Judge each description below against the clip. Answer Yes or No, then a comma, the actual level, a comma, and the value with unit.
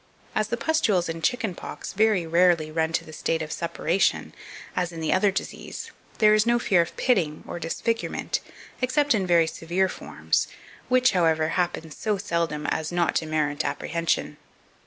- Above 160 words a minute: Yes, average, 175 wpm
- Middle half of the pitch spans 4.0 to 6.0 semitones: Yes, average, 4.7 semitones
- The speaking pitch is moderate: Yes, medium, 175 Hz